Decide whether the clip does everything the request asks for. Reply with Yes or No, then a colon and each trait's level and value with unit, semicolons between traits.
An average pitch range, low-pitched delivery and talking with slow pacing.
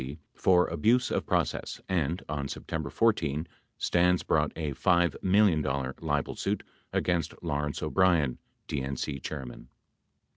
Yes: average, 3.8 semitones; very low, 80 Hz; slow, 120 wpm